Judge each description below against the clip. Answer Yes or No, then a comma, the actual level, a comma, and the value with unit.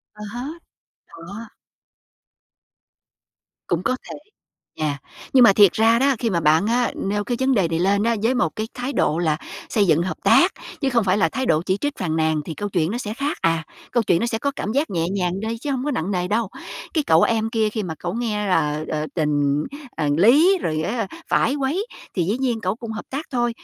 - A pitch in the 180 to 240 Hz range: Yes, high, 210 Hz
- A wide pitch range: Yes, wide, 6.1 semitones